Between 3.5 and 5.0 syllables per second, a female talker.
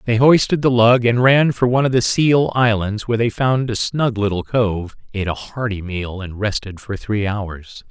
No: 4.8 syllables/s; male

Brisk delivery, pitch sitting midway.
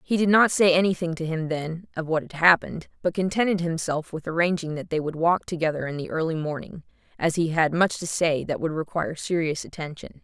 Yes: fast, 215 wpm; medium, 165 Hz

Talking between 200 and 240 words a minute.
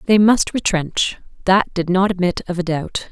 No: average, 190 wpm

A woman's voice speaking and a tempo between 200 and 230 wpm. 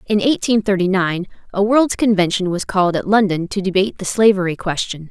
No: female; average, 190 wpm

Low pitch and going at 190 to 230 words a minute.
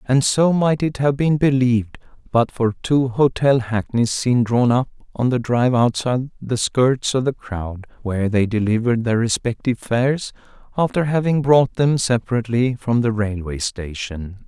No: low, 120 Hz; average, 160 wpm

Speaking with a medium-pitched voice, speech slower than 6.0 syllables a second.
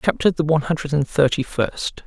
Yes: medium, 145 Hz; 5.6 syllables/s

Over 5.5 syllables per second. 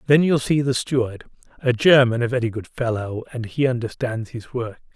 No: 5.2 syllables/s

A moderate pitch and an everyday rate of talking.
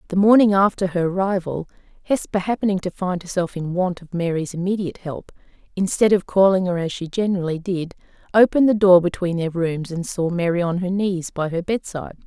Yes: medium, 180 Hz; average, 190 wpm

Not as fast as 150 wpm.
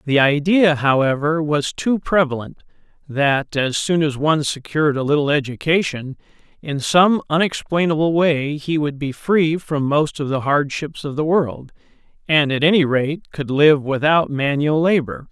No: average, 155 wpm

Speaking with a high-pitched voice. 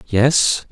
No: low, 125 Hz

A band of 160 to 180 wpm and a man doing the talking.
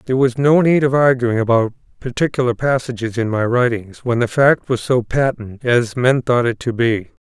No: average, 200 wpm; male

